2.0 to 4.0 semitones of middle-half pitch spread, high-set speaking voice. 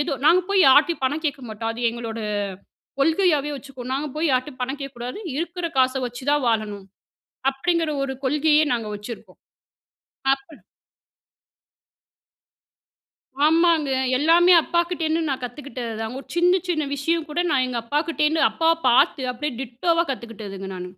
No: average, 4.8 semitones; very high, 280 Hz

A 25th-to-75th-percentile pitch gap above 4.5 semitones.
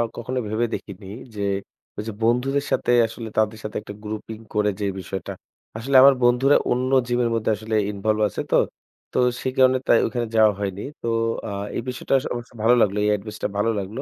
No: average, 2.7 semitones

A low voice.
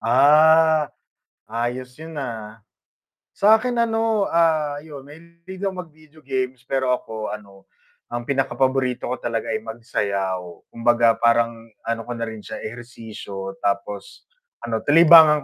Yes: low, 125 Hz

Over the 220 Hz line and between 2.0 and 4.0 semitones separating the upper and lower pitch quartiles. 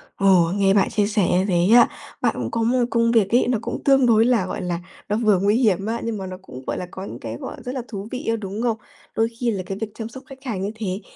No: high, 210 Hz; average, 3.4 semitones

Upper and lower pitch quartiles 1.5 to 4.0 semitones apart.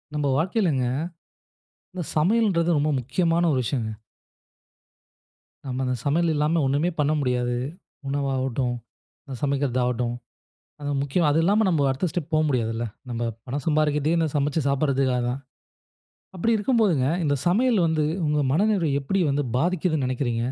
No: average, 4.4 semitones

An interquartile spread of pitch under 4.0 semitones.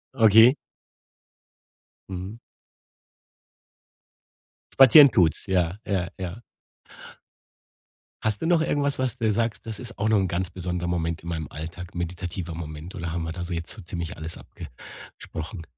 No: average, 4.6 semitones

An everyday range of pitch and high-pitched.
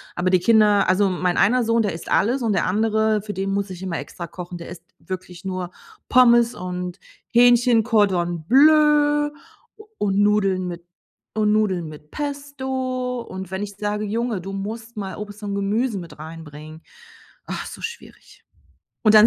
Yes: average, 4.3 semitones; high, 205 Hz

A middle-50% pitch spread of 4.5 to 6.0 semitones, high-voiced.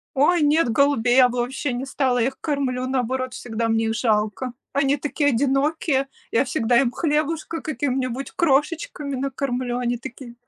No: average, 2.7 semitones; very high, 265 Hz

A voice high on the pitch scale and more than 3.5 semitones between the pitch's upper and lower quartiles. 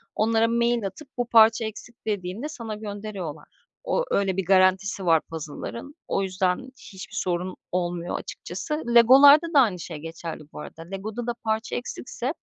Yes: high, 210 Hz; average, 4.5 semitones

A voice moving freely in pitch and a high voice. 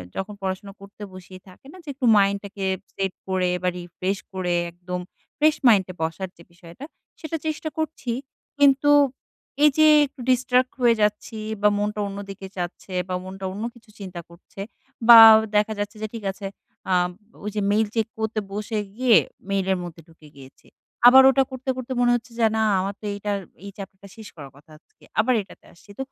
No: average, 4.2 semitones; high, 205 Hz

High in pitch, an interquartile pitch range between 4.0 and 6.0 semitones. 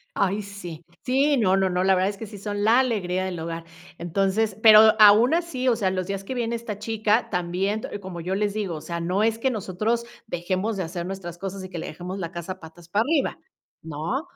No: high, 195 Hz; average, 3.6 semitones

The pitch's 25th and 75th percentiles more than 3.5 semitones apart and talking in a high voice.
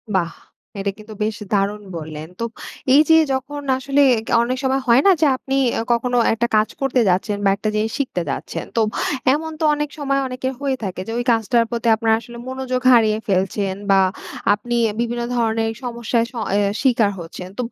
Yes: average, 3.9 semitones; high, 235 Hz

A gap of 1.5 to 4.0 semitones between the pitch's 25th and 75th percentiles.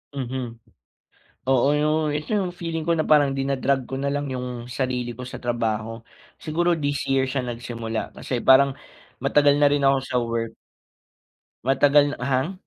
Yes: average, 2.8 semitones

